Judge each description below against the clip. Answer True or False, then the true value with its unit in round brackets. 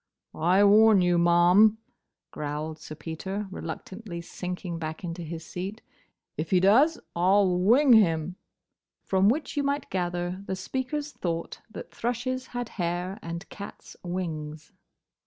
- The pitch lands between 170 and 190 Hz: True (185 Hz)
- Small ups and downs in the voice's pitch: False (4.2 semitones)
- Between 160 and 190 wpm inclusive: False (140 wpm)